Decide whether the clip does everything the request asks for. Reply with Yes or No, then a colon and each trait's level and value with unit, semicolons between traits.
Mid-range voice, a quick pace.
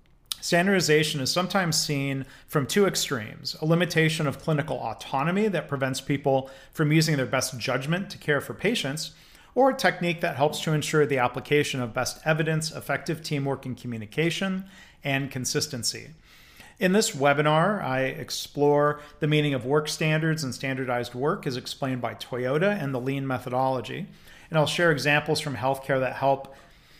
No: medium, 145 Hz; average, 160 wpm